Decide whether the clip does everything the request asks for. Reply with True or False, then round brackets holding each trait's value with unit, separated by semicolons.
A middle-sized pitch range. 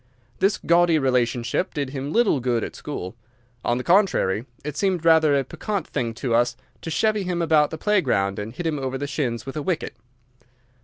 False (5.7 semitones)